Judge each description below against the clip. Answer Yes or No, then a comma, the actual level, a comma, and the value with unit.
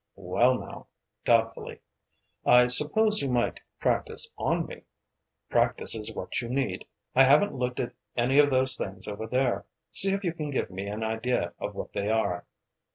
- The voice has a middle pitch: No, low, 125 Hz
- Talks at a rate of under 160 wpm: No, average, 170 wpm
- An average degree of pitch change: Yes, average, 3.5 semitones